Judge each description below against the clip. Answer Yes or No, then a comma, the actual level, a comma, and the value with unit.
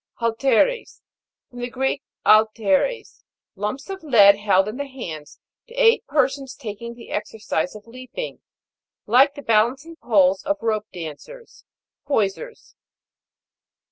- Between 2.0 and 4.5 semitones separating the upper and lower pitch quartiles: No, average, 5.2 semitones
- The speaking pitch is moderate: No, high, 235 Hz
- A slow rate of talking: Yes, slow, 125 wpm